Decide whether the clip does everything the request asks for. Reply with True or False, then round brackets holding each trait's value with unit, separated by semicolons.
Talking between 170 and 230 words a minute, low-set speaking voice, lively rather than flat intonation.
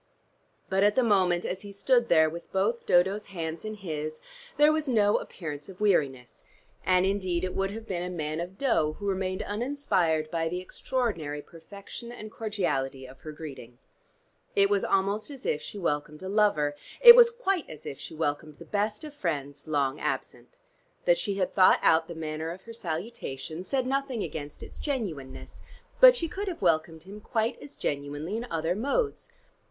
False (185 wpm; 185 Hz; 5.9 semitones)